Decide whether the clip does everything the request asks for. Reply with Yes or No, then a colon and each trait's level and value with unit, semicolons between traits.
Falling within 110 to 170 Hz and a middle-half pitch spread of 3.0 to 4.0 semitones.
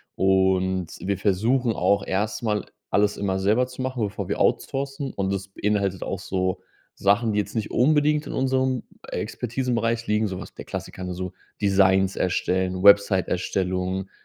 No: low, 100 Hz; average, 3.7 semitones